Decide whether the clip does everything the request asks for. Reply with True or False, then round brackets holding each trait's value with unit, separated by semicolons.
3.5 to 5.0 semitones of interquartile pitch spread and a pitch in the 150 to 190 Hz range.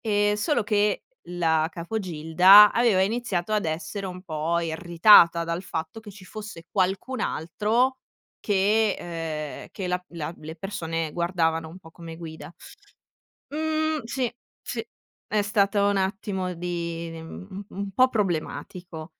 True (4.0 semitones; 185 Hz)